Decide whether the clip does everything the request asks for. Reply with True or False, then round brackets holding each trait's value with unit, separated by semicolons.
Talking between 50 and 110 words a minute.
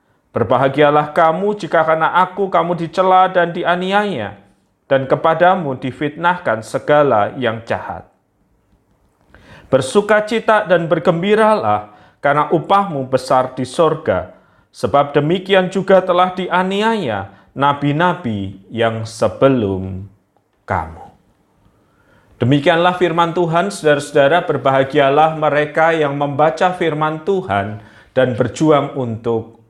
True (90 wpm)